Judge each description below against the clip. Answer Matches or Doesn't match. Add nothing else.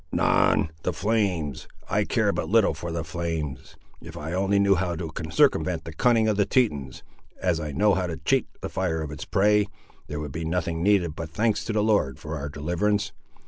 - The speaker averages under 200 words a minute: Doesn't match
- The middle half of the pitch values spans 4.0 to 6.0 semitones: Matches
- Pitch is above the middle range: Doesn't match